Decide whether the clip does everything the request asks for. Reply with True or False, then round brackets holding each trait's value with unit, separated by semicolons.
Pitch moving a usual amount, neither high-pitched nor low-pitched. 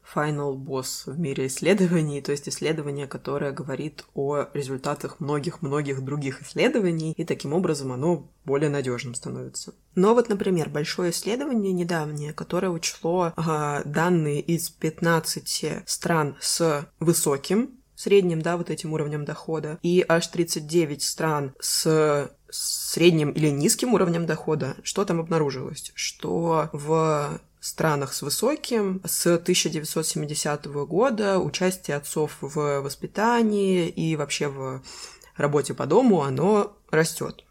True (3.3 semitones; 160 Hz)